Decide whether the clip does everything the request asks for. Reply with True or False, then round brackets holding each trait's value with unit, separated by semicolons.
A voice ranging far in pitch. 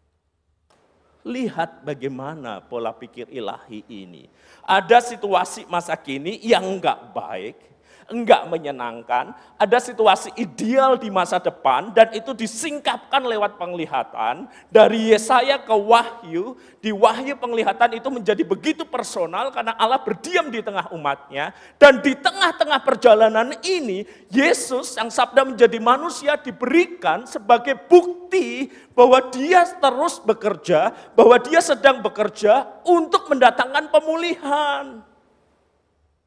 True (7.1 semitones)